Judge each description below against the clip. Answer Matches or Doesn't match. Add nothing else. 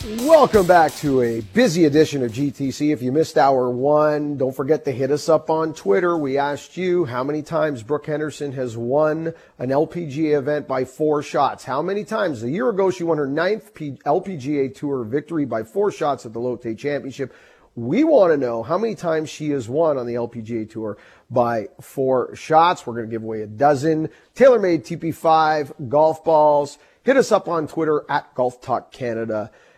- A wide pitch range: Doesn't match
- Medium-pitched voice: Matches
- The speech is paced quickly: Doesn't match